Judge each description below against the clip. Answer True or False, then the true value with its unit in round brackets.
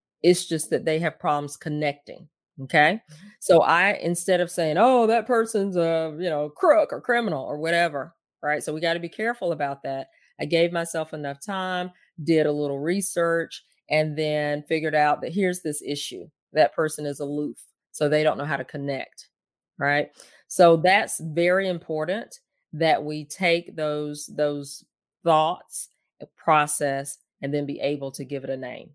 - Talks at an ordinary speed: True (170 wpm)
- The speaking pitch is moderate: True (155 Hz)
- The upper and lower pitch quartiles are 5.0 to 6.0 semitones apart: False (2.8 semitones)